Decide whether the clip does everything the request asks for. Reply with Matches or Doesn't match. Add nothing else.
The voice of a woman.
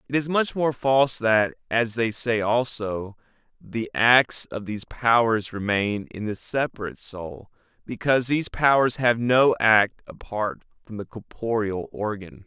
Doesn't match